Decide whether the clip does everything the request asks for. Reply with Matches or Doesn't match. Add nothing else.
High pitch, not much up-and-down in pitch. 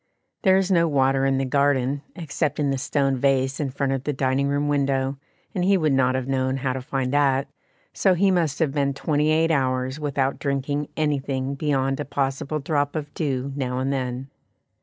Doesn't match